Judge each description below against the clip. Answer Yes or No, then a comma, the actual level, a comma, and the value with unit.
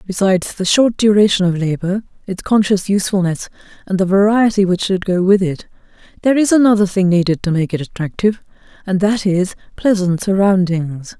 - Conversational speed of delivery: Yes, average, 165 wpm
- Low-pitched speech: No, high, 190 Hz